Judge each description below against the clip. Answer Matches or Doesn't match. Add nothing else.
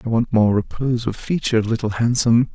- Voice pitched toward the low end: Matches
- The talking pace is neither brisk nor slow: Matches